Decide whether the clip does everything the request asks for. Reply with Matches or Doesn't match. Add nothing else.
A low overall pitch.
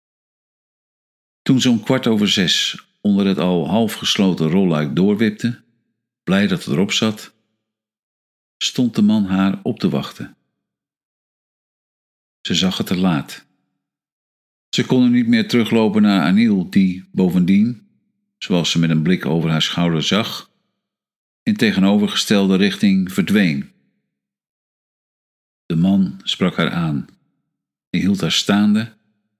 Matches